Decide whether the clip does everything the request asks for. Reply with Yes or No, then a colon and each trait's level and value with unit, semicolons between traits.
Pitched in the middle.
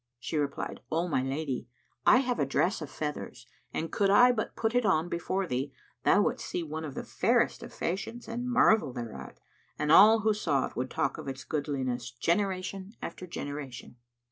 Yes: medium, 160 Hz